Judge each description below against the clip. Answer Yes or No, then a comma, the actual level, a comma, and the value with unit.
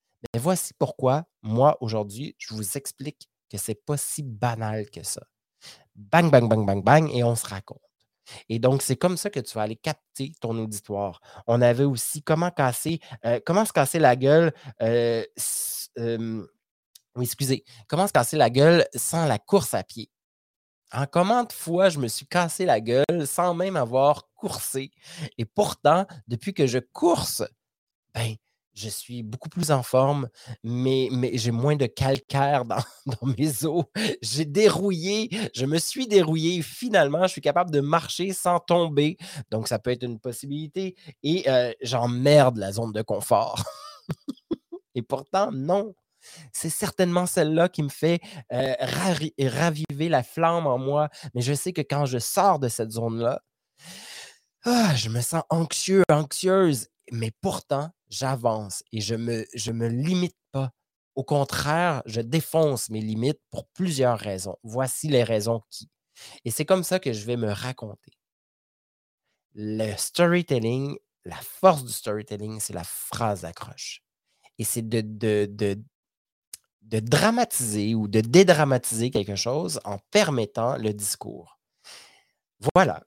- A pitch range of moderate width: No, wide, 5.9 semitones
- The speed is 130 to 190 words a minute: Yes, average, 155 wpm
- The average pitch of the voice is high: No, low, 135 Hz